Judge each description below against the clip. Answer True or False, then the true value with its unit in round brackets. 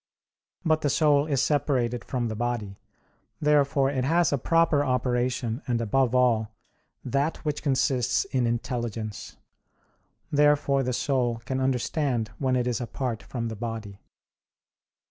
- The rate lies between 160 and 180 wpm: False (135 wpm)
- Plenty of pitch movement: False (3.2 semitones)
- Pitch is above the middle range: False (125 Hz)